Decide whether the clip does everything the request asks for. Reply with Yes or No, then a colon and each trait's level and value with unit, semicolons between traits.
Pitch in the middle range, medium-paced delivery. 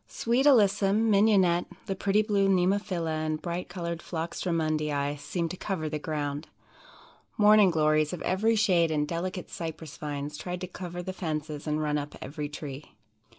Yes: medium, 170 Hz; average, 160 wpm